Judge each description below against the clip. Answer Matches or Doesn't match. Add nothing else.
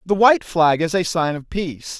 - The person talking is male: Matches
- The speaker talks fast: Matches